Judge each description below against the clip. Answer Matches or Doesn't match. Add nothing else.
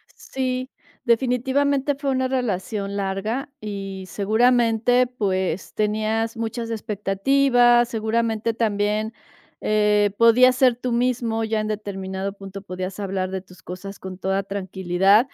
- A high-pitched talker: Matches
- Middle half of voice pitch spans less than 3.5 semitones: Doesn't match